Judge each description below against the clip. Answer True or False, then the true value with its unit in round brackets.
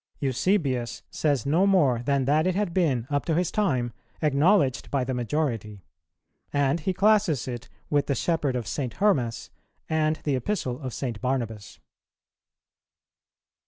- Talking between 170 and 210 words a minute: False (145 wpm)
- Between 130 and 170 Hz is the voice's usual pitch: True (140 Hz)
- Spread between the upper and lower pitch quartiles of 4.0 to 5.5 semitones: True (4.9 semitones)